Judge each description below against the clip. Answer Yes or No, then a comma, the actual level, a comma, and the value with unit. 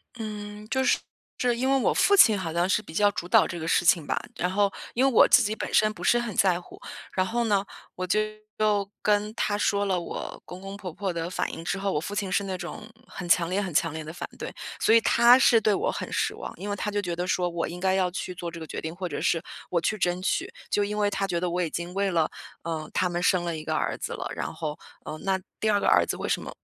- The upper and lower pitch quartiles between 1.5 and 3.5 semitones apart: Yes, average, 3.1 semitones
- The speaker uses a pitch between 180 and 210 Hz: Yes, high, 190 Hz